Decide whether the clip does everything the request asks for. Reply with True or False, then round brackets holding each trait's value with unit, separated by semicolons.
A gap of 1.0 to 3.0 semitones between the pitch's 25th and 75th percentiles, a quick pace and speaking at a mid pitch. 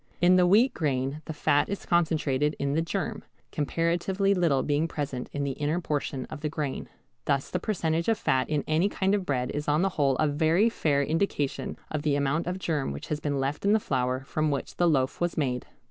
False (3.7 semitones; 220 wpm; 150 Hz)